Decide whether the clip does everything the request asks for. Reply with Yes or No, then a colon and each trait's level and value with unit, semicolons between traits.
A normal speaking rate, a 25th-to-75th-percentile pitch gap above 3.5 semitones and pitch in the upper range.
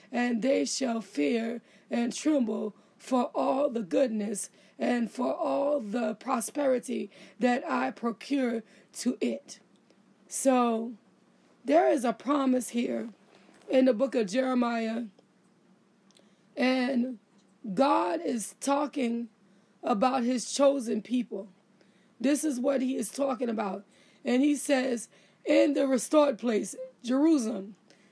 No: slow, 115 wpm; average, 4.1 semitones; high, 240 Hz